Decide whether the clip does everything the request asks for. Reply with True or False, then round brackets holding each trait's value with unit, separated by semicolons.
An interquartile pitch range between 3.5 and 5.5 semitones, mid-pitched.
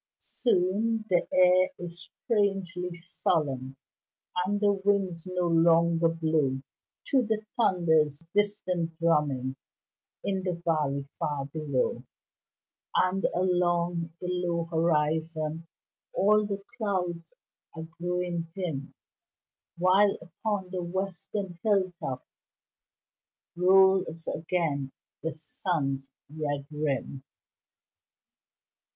False (3.0 semitones; 175 Hz)